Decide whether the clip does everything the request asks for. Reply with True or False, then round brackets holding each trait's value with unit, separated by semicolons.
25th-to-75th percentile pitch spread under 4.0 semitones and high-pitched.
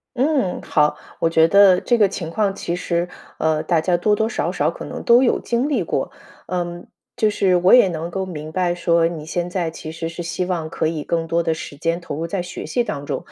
False (2.9 semitones; 175 Hz)